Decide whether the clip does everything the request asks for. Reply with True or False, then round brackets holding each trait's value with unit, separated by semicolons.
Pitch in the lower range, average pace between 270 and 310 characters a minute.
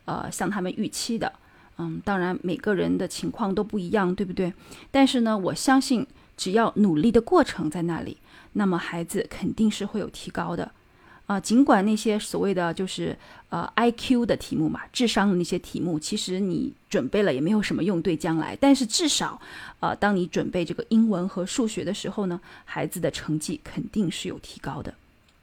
False (200 Hz; 290 characters per minute)